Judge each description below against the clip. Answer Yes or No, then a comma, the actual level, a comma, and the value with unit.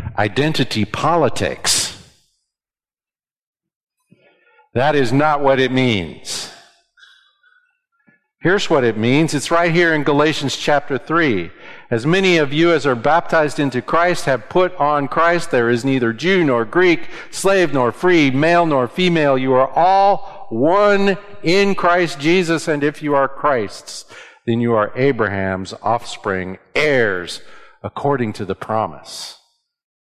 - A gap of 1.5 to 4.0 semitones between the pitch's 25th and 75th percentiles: No, wide, 5.6 semitones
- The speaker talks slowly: Yes, slow, 130 wpm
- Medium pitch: Yes, medium, 155 Hz